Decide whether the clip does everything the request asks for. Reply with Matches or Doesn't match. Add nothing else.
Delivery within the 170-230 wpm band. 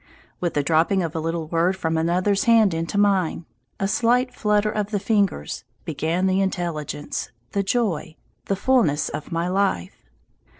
Doesn't match